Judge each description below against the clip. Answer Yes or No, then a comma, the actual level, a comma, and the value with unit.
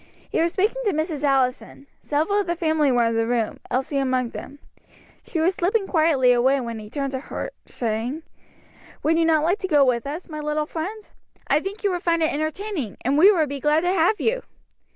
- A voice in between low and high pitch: No, very high, 305 Hz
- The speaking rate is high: Yes, fast, 215 wpm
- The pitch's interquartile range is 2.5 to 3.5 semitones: No, average, 4.8 semitones